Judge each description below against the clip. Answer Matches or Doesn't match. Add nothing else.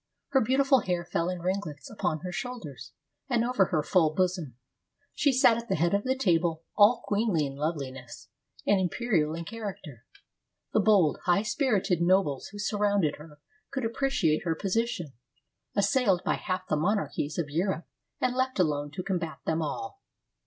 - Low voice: Doesn't match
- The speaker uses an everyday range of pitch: Doesn't match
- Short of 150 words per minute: Doesn't match